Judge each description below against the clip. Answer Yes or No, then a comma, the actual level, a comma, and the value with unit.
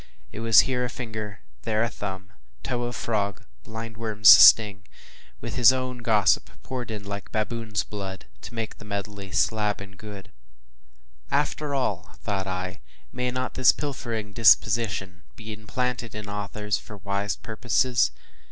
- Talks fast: No, average, 155 wpm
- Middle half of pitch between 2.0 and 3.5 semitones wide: Yes, average, 2.8 semitones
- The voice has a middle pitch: No, low, 110 Hz